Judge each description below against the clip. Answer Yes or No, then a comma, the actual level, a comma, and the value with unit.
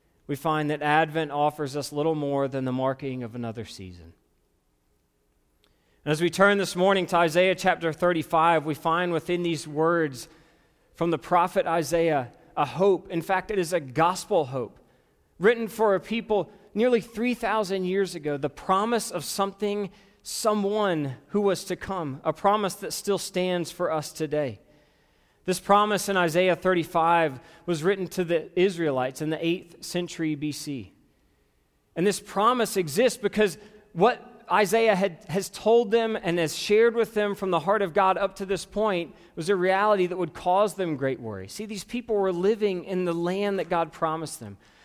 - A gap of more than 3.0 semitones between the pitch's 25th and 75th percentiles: Yes, average, 4.3 semitones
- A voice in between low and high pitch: Yes, medium, 175 Hz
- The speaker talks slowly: No, average, 170 wpm